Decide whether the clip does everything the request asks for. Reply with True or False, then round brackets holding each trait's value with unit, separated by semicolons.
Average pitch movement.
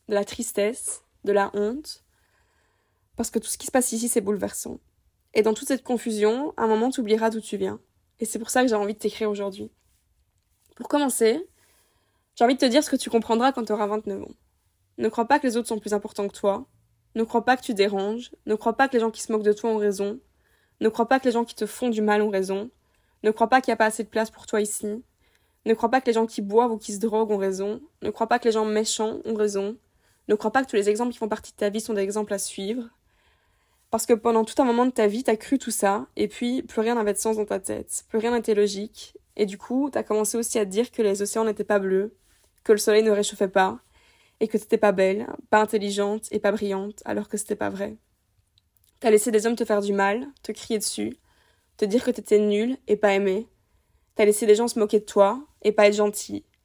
False (2.3 semitones)